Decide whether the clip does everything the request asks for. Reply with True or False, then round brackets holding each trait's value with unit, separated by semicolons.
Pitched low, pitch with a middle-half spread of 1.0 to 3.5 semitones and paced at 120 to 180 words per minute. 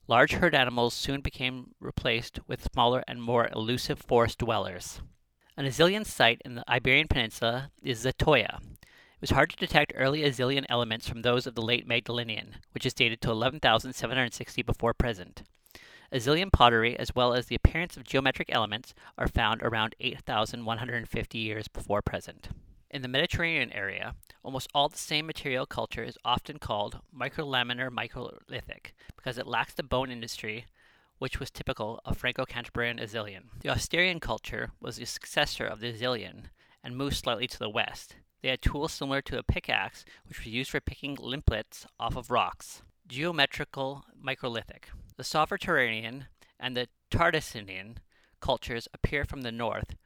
True (125 Hz; 3.0 semitones; 155 wpm)